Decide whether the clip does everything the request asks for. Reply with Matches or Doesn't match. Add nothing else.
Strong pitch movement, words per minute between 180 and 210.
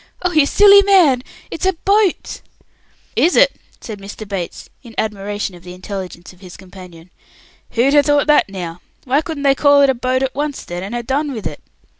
Matches